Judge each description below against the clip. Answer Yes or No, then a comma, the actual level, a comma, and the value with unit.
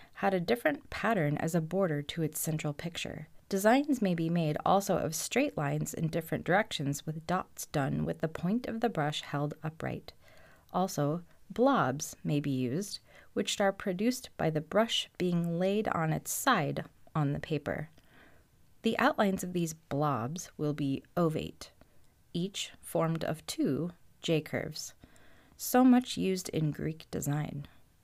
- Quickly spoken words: No, average, 155 wpm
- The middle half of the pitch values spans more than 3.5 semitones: Yes, average, 4.6 semitones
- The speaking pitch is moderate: Yes, medium, 160 Hz